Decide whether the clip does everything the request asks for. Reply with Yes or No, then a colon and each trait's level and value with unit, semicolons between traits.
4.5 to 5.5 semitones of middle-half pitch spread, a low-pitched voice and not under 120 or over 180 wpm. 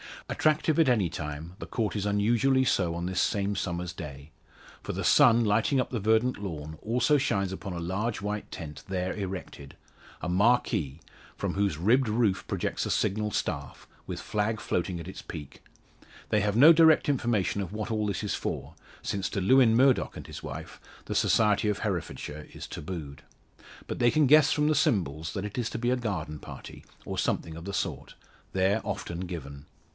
No: average, 5.2 semitones; low, 100 Hz; average, 190 wpm